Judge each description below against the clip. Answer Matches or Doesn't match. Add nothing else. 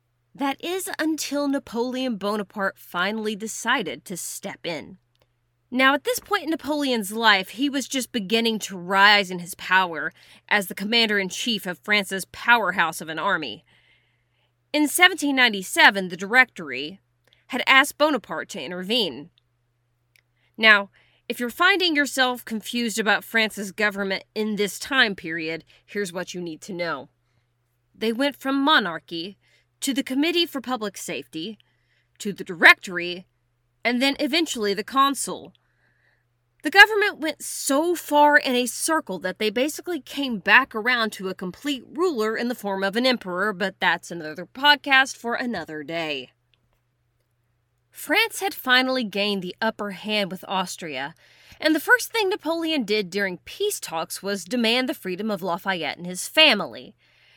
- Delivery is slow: Doesn't match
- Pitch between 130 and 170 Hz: Doesn't match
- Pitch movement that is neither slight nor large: Doesn't match